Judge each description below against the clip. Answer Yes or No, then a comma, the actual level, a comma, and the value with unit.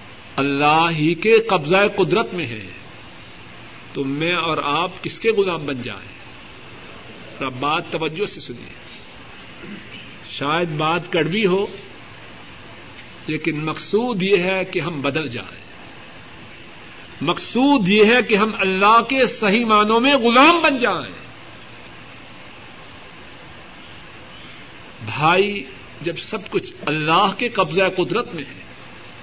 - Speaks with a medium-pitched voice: Yes, medium, 180 Hz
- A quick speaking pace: No, average, 115 wpm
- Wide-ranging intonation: Yes, wide, 5.9 semitones